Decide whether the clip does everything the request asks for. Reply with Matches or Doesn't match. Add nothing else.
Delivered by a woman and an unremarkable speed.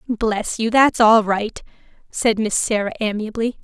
Matches